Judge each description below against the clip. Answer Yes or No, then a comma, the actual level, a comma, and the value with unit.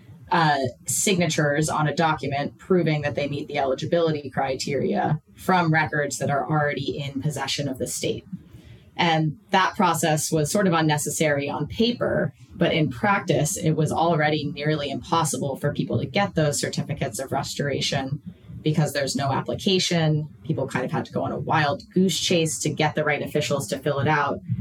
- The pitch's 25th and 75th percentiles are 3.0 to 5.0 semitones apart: No, narrow, 2.5 semitones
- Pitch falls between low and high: Yes, medium, 155 Hz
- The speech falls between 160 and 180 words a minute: Yes, average, 175 wpm